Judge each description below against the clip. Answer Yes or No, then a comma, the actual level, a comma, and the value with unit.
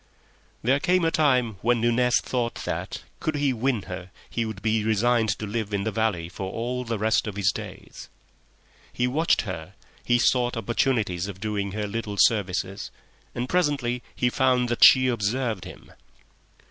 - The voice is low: Yes, low, 115 Hz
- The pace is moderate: Yes, average, 170 wpm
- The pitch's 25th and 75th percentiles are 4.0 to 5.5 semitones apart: No, average, 3.5 semitones